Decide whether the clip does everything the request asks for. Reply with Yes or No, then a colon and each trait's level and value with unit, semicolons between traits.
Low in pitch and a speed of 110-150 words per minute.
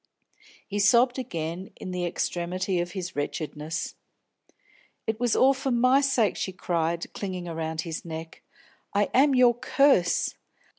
No: medium, 185 Hz; average, 140 wpm